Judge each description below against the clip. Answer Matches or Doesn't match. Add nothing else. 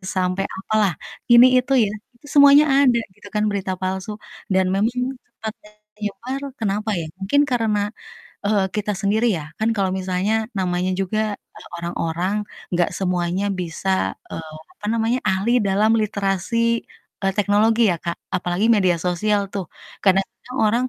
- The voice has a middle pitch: Doesn't match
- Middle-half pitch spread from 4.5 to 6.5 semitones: Doesn't match